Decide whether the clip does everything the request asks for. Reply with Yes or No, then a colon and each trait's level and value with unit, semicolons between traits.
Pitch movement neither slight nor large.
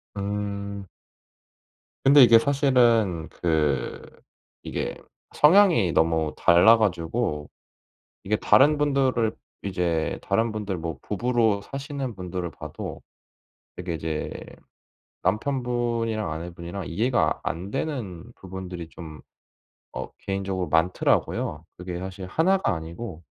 No: wide, 5.7 semitones